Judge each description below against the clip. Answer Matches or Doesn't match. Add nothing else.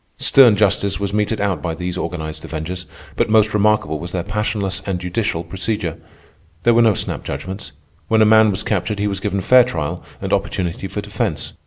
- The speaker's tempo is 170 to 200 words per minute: Matches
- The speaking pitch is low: Matches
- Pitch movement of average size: Matches